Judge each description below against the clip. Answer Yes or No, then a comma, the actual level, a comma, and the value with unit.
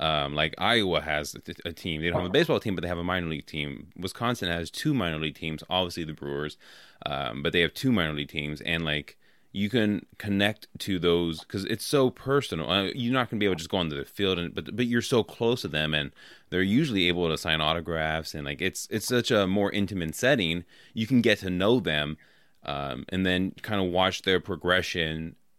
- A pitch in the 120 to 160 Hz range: No, very low, 90 Hz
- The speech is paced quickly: Yes, fast, 235 wpm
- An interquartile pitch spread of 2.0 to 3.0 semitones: No, average, 4.4 semitones